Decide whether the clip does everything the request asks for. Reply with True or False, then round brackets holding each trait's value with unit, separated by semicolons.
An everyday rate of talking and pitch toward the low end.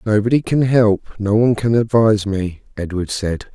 True (170 wpm; 105 Hz)